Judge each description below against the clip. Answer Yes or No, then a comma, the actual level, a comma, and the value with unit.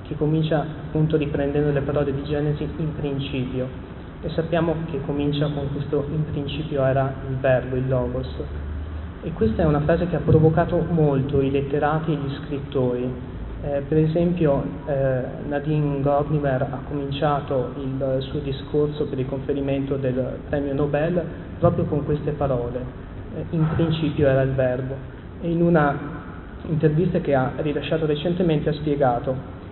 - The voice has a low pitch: No, medium, 145 Hz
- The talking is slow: No, average, 150 wpm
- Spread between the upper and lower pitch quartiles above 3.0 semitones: No, narrow, 2.4 semitones